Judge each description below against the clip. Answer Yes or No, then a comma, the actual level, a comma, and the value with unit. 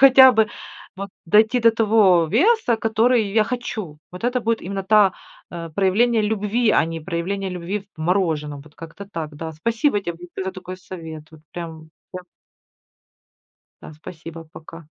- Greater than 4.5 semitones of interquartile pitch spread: Yes, average, 5.1 semitones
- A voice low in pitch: No, high, 190 Hz